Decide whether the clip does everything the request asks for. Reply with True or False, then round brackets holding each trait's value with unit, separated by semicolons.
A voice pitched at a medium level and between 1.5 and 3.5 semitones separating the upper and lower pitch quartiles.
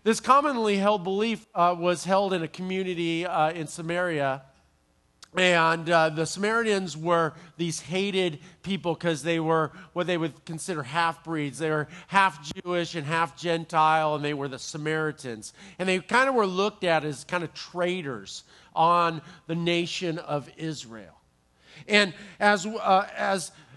True (170 Hz; 3.1 semitones)